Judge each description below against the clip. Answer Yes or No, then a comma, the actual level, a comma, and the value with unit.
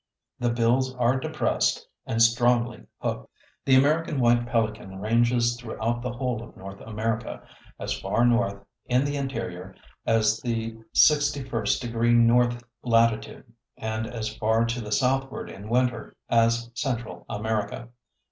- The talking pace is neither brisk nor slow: No, slow, 130 wpm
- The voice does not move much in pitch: Yes, narrow, 1.7 semitones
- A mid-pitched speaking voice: No, low, 115 Hz